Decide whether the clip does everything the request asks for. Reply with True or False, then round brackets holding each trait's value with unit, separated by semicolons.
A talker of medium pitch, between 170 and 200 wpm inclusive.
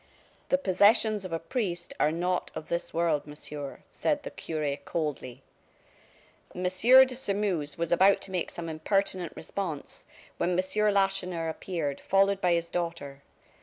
False (175 Hz; 145 wpm)